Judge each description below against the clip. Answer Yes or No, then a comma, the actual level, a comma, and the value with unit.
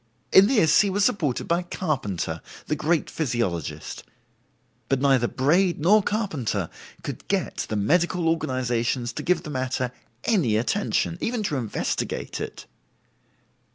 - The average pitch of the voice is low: No, medium, 150 Hz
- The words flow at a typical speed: No, slow, 130 wpm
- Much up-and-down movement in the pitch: Yes, wide, 7.0 semitones